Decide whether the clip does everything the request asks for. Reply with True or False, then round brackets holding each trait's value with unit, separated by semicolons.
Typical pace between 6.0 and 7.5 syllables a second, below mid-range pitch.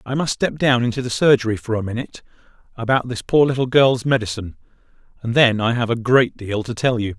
True (6.1 syllables/s; 120 Hz)